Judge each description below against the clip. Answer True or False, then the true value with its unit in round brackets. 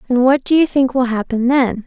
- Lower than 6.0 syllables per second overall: True (5.3 syllables/s)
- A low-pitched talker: False (255 Hz)